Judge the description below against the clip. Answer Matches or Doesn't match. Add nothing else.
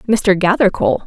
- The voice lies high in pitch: Matches